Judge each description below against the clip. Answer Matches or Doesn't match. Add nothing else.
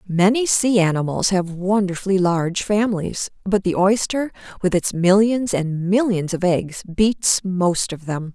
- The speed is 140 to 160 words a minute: Matches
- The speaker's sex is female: Matches